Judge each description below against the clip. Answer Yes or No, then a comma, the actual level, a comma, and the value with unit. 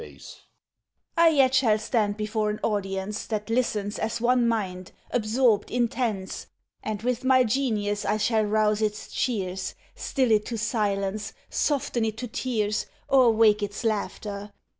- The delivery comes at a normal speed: Yes, average, 155 wpm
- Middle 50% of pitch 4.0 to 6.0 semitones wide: No, average, 2.7 semitones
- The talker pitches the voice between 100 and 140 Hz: No, high, 215 Hz